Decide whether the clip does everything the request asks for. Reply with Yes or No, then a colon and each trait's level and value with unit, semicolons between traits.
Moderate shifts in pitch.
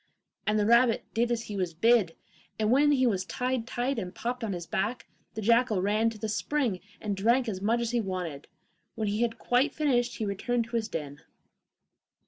Yes: average, 3.5 semitones